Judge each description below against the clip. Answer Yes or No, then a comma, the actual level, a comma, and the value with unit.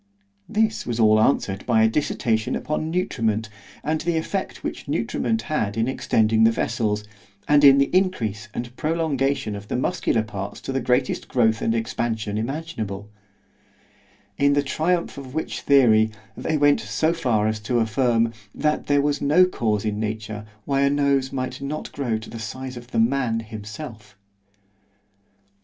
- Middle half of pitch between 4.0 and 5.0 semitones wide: Yes, average, 4.6 semitones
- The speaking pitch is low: Yes, low, 120 Hz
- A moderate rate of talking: Yes, average, 160 wpm